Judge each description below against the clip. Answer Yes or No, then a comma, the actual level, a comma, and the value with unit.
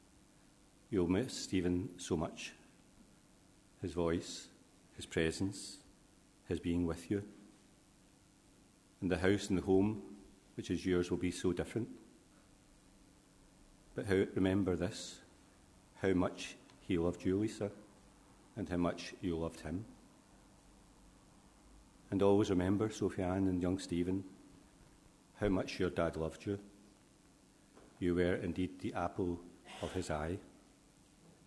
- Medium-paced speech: No, slow, 120 wpm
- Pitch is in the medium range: No, very low, 95 Hz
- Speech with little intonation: Yes, narrow, 2.1 semitones